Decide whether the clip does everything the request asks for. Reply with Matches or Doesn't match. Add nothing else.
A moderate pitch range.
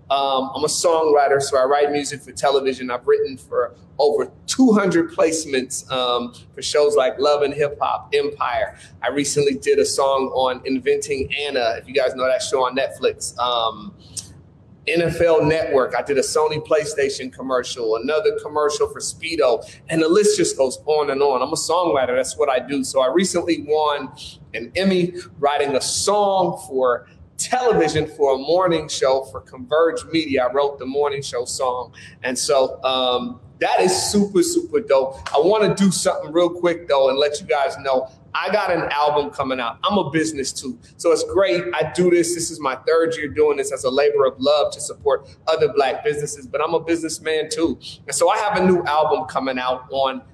Doesn't match